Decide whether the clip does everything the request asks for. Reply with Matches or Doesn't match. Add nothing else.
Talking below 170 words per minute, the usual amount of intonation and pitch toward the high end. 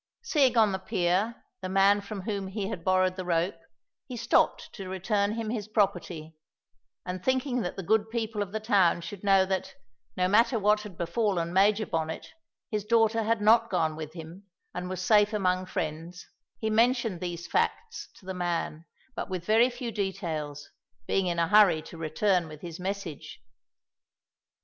Doesn't match